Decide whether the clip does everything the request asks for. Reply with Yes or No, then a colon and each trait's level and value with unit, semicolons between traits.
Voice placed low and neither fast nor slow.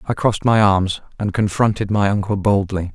Yes: low, 100 Hz; average, 185 wpm